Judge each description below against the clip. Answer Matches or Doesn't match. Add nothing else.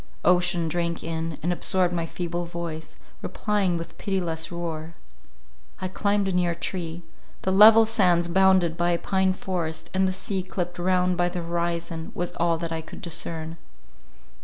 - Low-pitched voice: Doesn't match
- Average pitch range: Doesn't match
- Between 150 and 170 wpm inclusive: Matches